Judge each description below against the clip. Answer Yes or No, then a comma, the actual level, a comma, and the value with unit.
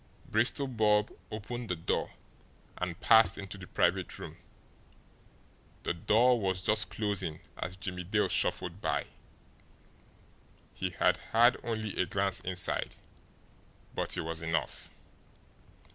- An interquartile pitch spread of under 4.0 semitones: Yes, average, 3.4 semitones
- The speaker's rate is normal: No, slow, 120 wpm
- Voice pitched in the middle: No, low, 100 Hz